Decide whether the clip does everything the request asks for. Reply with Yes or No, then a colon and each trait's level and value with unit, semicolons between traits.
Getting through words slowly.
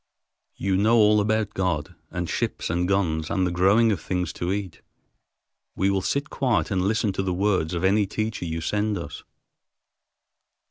No: average, 175 wpm